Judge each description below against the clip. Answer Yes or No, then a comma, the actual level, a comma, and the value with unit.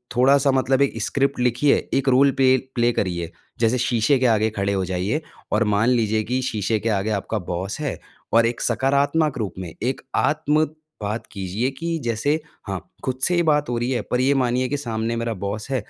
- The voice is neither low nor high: No, low, 120 Hz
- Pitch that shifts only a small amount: No, average, 4.1 semitones